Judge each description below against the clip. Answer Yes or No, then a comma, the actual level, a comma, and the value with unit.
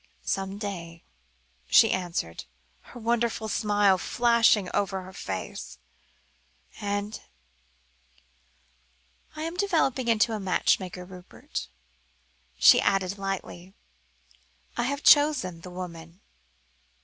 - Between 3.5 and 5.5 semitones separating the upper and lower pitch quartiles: Yes, average, 4.3 semitones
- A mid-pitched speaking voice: No, high, 200 Hz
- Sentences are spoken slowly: Yes, slow, 100 wpm